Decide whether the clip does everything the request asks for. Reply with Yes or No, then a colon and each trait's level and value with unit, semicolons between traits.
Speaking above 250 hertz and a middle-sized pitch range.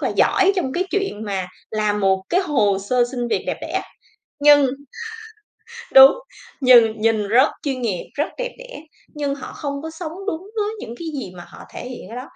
No: very high, 265 Hz; wide, 6.6 semitones